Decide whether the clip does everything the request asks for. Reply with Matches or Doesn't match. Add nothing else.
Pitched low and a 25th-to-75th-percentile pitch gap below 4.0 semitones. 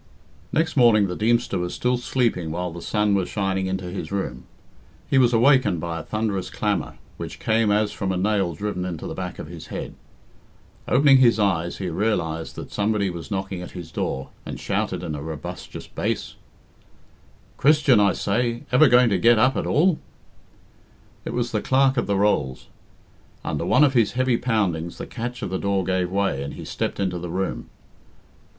Doesn't match